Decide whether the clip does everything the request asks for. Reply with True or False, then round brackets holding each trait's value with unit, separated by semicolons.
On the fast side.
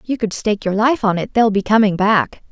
True (265 wpm)